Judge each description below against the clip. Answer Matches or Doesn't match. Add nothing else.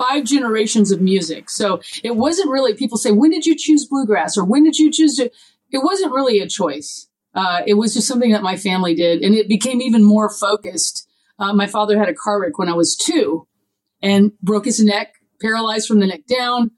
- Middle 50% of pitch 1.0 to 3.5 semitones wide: Doesn't match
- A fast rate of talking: Matches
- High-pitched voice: Matches